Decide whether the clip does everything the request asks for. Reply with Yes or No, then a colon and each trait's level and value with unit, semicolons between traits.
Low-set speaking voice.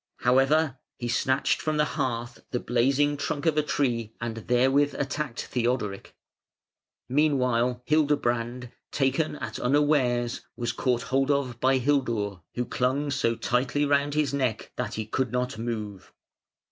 Yes: low, 130 Hz